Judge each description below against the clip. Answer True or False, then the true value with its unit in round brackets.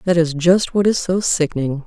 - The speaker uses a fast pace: True (225 wpm)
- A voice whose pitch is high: False (170 Hz)